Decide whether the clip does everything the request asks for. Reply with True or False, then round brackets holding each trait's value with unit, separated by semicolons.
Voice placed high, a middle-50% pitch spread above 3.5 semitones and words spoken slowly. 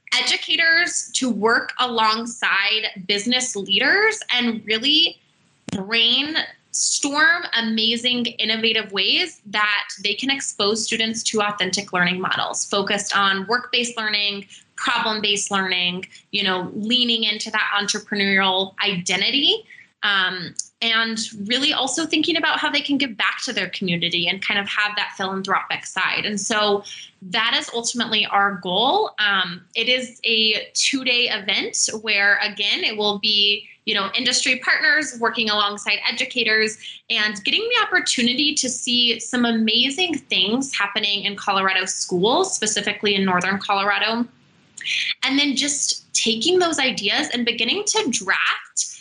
True (220 Hz; 3.9 semitones; 130 wpm)